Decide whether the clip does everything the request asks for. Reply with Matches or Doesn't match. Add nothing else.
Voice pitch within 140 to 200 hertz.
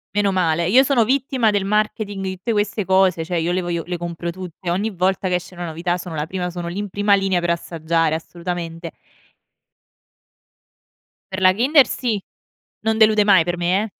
Matches